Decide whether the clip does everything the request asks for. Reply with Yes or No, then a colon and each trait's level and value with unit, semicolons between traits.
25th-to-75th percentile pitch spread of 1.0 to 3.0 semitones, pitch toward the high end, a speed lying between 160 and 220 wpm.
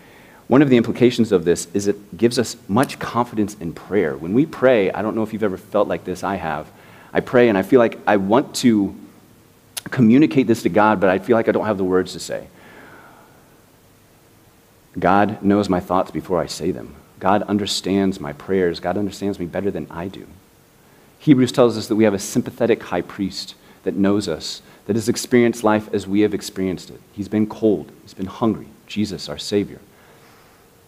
No: narrow, 2.6 semitones; low, 100 Hz; average, 200 wpm